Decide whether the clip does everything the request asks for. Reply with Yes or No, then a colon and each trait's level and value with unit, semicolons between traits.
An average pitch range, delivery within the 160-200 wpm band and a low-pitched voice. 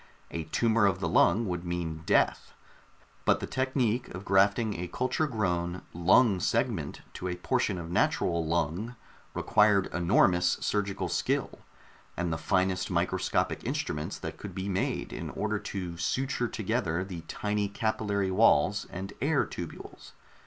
No: average, 3.6 semitones; average, 145 wpm; very low, 95 Hz